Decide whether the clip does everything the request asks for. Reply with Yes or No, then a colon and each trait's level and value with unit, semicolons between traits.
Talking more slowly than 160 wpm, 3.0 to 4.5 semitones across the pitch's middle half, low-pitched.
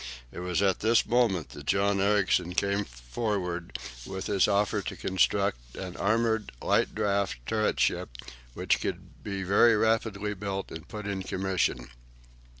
No: average, 150 wpm; narrow, 2.4 semitones; low, 100 Hz